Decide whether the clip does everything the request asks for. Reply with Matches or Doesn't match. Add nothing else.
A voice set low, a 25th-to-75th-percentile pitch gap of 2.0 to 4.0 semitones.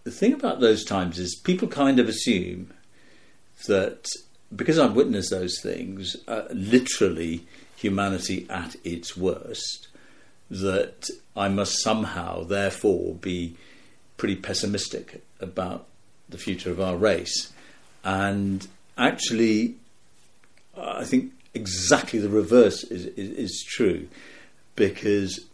Matches